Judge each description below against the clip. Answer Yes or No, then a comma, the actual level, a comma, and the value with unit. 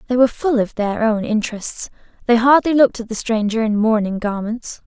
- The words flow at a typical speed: Yes, average, 195 wpm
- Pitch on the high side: Yes, high, 225 Hz